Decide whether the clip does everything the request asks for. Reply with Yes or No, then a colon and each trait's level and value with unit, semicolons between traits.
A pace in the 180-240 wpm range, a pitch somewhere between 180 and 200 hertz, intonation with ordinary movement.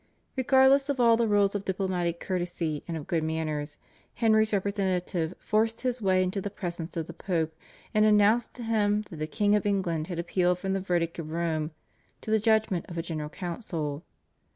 Yes: average, 190 wpm; medium, 185 Hz; average, 4.2 semitones